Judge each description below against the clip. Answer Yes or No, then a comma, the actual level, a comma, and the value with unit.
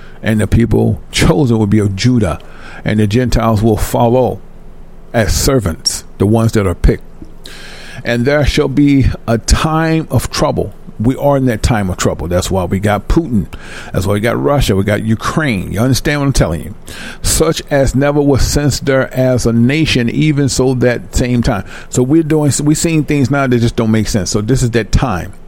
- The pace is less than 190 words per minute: No, average, 200 wpm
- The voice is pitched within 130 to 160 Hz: No, low, 120 Hz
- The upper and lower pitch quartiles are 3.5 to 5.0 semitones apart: Yes, average, 4.5 semitones